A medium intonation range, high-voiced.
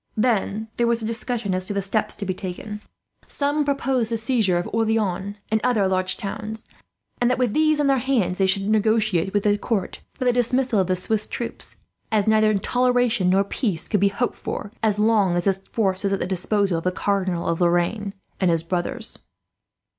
Yes: average, 3.4 semitones; high, 210 Hz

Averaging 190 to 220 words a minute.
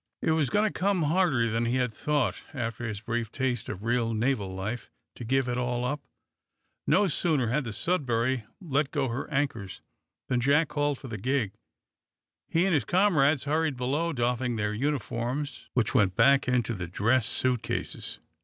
No: average, 180 wpm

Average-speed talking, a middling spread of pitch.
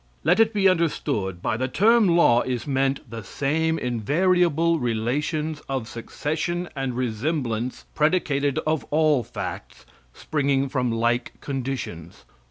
No: slow, 125 wpm; average, 4.9 semitones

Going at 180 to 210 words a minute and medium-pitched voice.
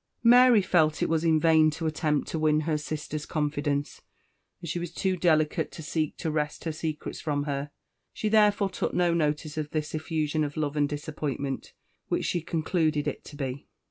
Yes: average, 190 wpm; medium, 155 Hz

